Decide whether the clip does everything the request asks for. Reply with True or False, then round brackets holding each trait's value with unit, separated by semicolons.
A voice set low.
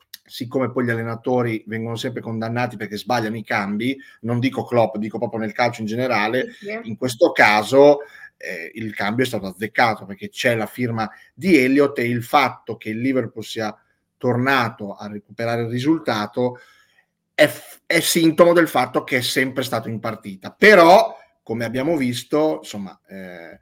True (120 Hz)